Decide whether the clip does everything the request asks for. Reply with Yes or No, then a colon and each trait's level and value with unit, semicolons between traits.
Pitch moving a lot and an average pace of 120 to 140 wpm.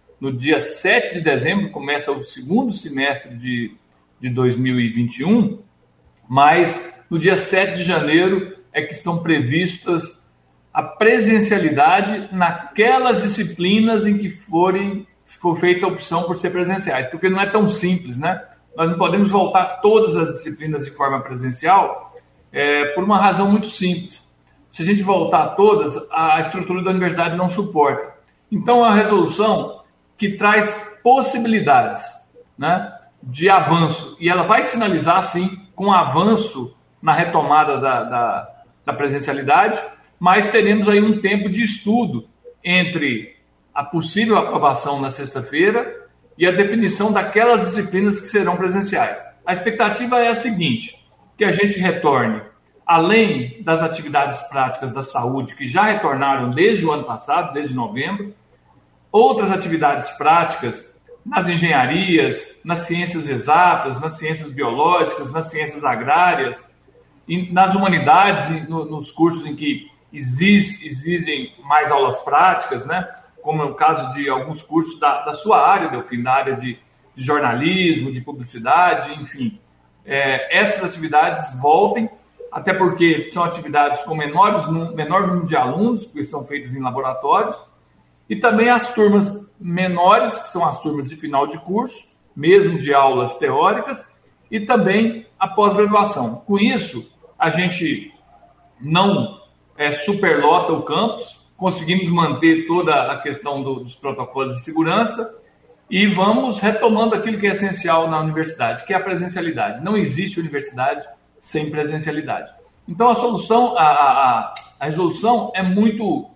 Yes: wide, 5.7 semitones; average, 135 wpm